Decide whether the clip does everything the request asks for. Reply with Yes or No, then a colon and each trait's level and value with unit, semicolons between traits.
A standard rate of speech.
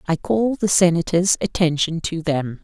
Yes: average, 160 wpm